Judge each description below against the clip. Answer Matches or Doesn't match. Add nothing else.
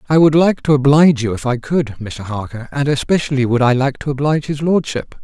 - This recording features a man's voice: Matches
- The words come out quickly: Matches